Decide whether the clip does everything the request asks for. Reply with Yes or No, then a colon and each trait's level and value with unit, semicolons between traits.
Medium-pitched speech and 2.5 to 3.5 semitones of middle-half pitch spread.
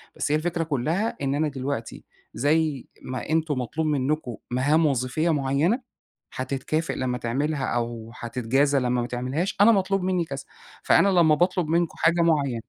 No: medium, 145 Hz; average, 4.3 semitones